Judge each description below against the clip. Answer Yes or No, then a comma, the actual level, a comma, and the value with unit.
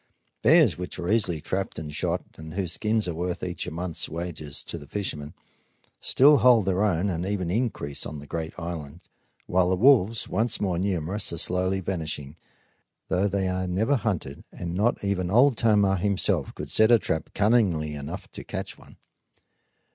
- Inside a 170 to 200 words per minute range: Yes, average, 180 wpm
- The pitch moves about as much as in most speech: Yes, average, 3.9 semitones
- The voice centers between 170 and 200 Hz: No, very low, 90 Hz